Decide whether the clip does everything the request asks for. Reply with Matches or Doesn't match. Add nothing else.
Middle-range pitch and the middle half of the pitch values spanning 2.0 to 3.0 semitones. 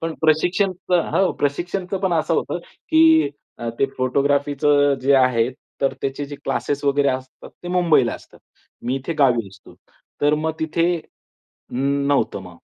Doesn't match